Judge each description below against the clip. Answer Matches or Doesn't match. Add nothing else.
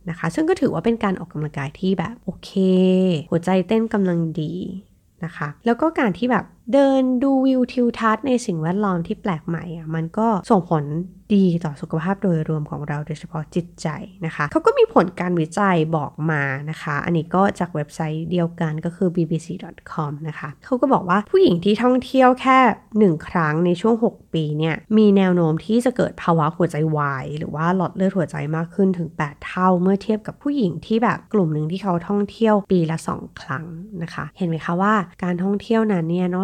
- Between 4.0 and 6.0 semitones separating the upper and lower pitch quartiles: Matches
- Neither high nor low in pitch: Matches